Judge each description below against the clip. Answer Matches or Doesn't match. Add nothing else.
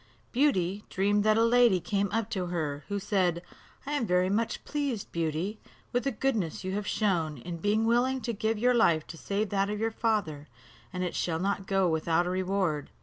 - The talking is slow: Doesn't match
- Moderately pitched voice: Doesn't match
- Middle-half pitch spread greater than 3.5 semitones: Matches